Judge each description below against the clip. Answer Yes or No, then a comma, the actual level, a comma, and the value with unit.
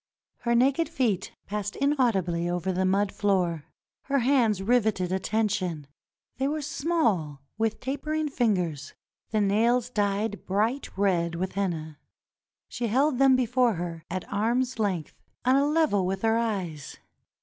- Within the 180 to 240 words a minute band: No, average, 140 wpm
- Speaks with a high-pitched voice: Yes, high, 210 Hz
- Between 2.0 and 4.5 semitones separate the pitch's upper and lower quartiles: No, average, 5.2 semitones